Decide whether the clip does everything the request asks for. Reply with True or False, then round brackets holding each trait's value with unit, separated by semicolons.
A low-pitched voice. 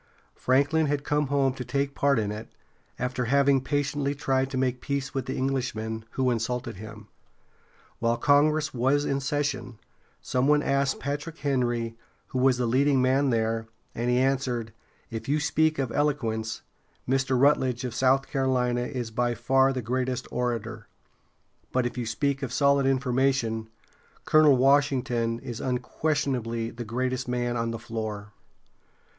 True (130 Hz)